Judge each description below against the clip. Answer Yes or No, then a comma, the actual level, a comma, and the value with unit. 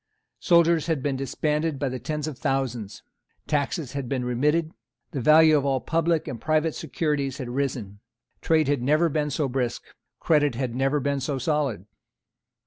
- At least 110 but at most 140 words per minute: No, average, 160 wpm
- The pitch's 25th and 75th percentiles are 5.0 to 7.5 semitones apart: No, average, 3.0 semitones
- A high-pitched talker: No, medium, 140 Hz